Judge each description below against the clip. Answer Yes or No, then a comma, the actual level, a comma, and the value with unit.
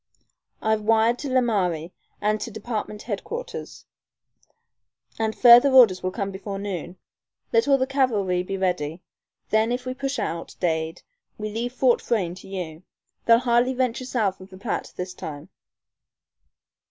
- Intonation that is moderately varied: Yes, average, 4.7 semitones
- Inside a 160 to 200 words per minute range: No, average, 150 wpm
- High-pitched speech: Yes, high, 215 Hz